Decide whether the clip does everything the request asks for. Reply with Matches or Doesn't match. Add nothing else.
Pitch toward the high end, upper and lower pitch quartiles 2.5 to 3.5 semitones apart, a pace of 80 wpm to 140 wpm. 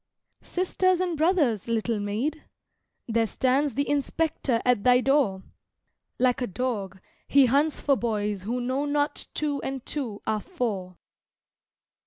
Doesn't match